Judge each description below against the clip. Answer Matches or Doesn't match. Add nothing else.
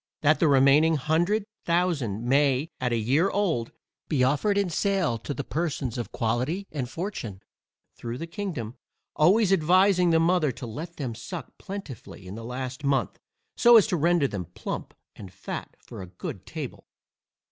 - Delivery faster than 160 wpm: Matches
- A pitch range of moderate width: Doesn't match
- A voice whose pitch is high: Doesn't match